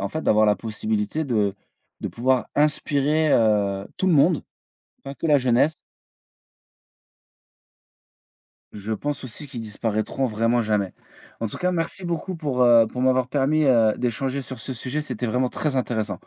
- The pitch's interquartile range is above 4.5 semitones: Yes, average, 5.1 semitones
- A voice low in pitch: Yes, low, 130 Hz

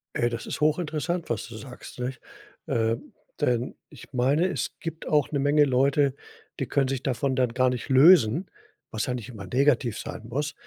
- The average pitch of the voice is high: No, low, 130 Hz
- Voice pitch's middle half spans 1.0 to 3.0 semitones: No, average, 3.5 semitones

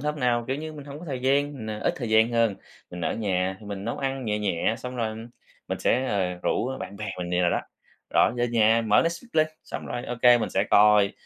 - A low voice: Yes, low, 115 Hz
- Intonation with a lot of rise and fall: No, average, 4.4 semitones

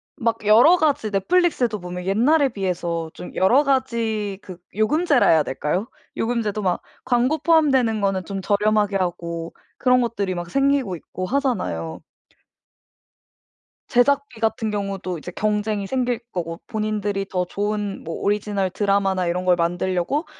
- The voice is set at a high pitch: Yes, high, 205 Hz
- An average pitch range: Yes, average, 4.9 semitones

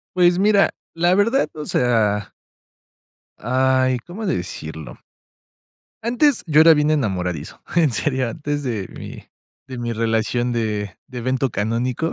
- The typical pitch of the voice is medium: No, low, 130 Hz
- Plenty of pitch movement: Yes, wide, 6.4 semitones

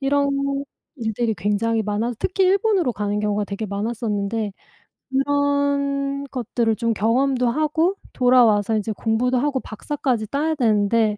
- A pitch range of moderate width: Yes, average, 4.7 semitones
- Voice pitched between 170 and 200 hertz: No, high, 240 Hz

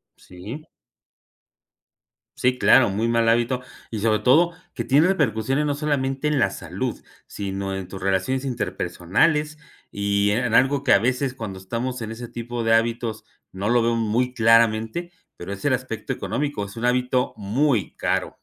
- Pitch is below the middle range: Yes, low, 115 Hz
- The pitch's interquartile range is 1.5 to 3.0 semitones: No, average, 3.8 semitones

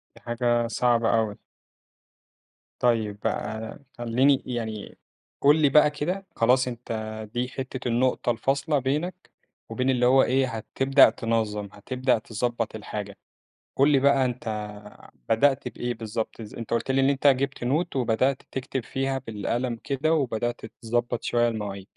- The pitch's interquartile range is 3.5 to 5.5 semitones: No, average, 2.9 semitones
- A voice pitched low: Yes, low, 125 Hz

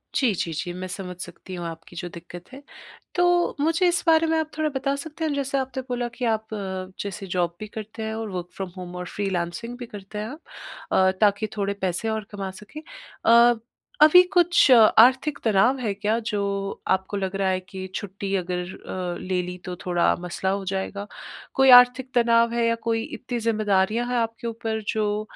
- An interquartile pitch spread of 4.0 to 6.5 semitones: Yes, average, 4.4 semitones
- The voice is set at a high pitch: Yes, high, 215 Hz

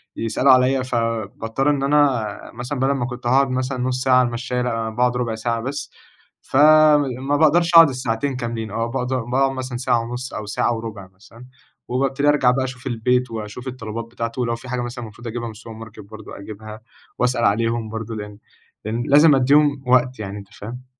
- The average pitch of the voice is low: Yes, low, 125 Hz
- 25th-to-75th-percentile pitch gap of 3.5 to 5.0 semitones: No, narrow, 2.5 semitones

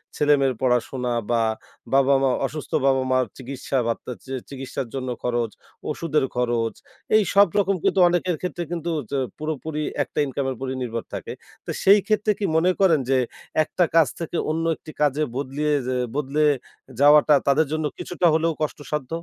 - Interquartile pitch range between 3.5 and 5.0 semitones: Yes, average, 3.8 semitones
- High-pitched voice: No, medium, 145 Hz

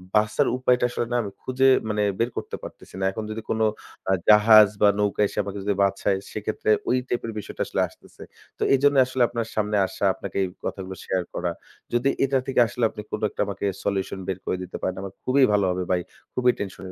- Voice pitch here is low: Yes, low, 105 Hz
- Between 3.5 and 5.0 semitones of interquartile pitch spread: Yes, average, 3.8 semitones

